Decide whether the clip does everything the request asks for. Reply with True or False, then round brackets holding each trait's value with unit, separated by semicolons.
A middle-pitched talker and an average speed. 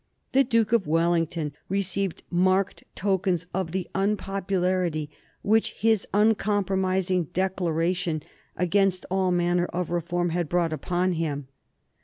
False (180 Hz; 115 wpm)